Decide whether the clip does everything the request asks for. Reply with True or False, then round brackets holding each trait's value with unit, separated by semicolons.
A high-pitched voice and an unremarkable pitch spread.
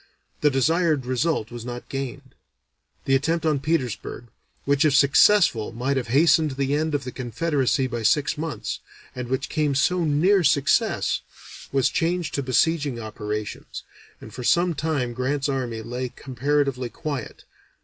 False (140 Hz; 3.7 semitones)